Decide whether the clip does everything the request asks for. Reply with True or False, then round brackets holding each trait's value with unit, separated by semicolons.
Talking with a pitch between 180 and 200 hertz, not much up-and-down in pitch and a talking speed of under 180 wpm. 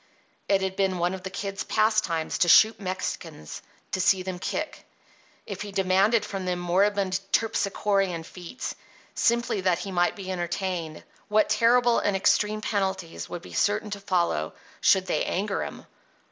True (190 Hz; 2.3 semitones; 160 wpm)